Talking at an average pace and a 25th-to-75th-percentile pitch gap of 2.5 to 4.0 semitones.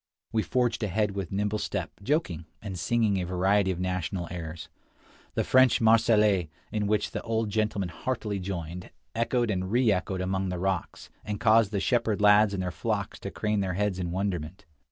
Yes: average, 175 wpm; average, 2.9 semitones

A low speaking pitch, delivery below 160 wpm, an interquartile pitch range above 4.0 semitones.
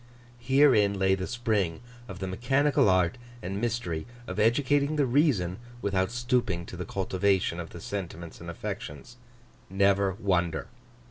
Yes: low, 100 Hz; average, 140 wpm; average, 5.0 semitones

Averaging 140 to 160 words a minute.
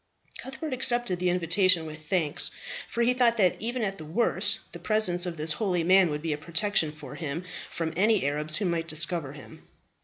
No: average, 195 wpm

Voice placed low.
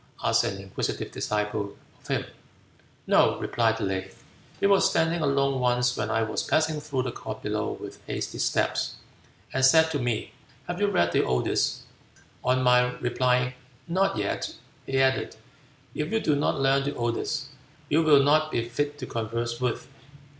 Yes: low, 130 Hz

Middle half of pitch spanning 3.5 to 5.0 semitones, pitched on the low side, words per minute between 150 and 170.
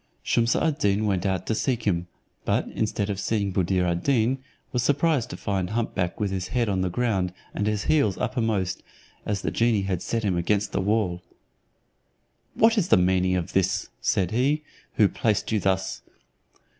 No: average, 3.8 semitones; low, 100 Hz; average, 185 wpm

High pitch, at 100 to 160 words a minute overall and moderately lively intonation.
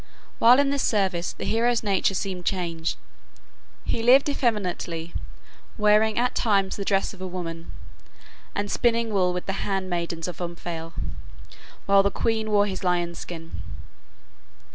Yes: high, 195 Hz; average, 145 wpm; average, 3.9 semitones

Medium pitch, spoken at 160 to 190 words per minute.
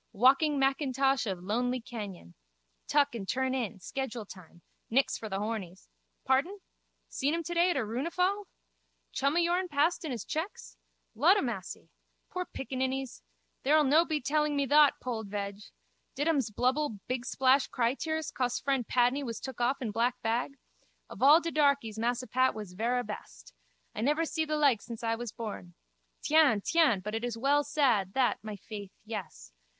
No: very high, 255 Hz; average, 165 wpm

